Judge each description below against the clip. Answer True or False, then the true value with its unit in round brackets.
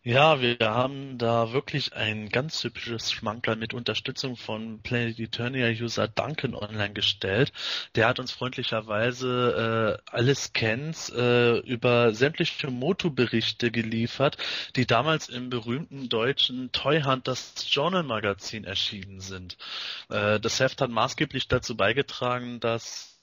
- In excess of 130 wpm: False (125 wpm)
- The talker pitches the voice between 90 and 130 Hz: True (120 Hz)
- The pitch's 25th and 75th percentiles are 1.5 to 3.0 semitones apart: True (2.7 semitones)